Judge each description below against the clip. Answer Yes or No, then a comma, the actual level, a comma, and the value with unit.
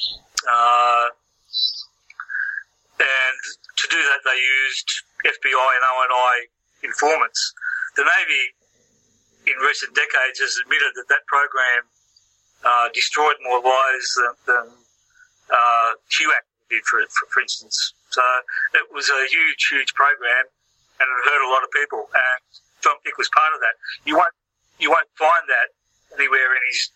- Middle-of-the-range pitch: No, low, 125 Hz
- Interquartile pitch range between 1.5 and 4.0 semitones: Yes, average, 2.7 semitones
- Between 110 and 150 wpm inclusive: Yes, average, 140 wpm